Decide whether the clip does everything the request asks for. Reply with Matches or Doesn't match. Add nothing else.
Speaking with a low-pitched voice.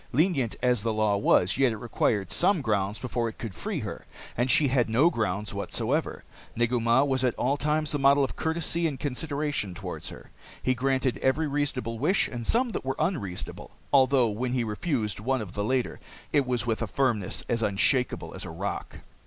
Matches